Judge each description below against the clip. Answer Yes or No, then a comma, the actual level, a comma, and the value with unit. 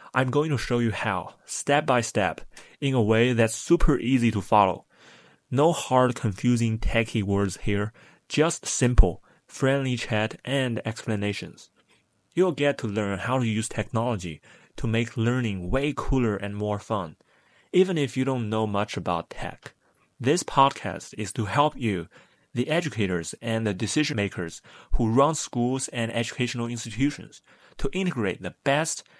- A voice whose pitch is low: Yes, low, 120 Hz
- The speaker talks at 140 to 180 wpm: Yes, average, 155 wpm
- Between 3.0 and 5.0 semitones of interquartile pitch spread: Yes, average, 4.2 semitones